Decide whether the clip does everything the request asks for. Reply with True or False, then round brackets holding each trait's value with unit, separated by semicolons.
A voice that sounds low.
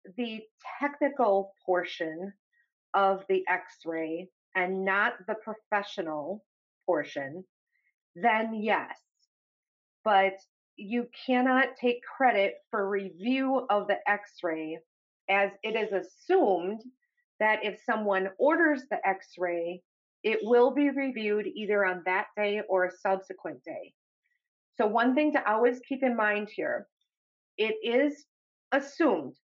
False (210 Hz)